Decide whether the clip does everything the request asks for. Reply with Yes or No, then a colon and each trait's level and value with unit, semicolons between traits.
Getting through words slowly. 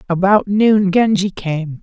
Yes: slow, 130 wpm